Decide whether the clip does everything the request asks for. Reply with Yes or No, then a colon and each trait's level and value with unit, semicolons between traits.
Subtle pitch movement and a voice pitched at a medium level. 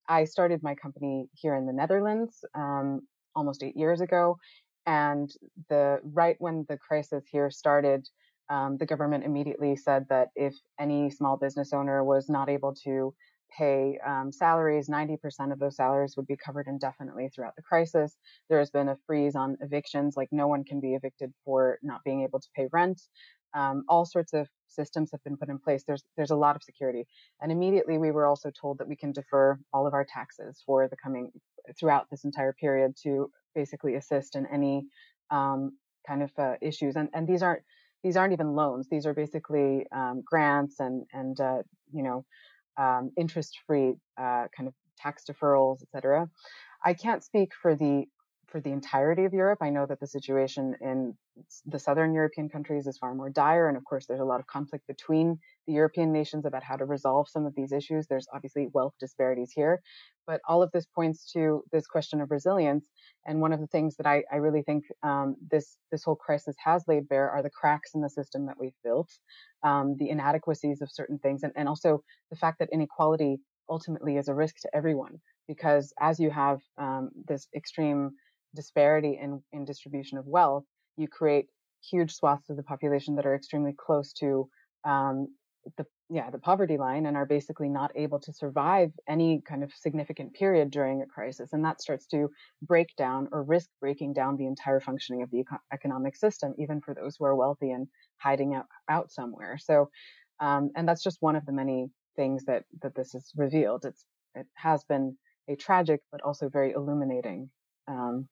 Yes: narrow, 2.1 semitones; medium, 145 Hz